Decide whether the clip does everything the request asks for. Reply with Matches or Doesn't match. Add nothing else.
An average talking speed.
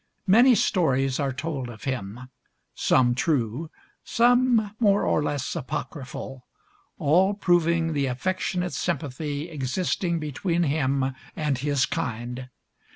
Doesn't match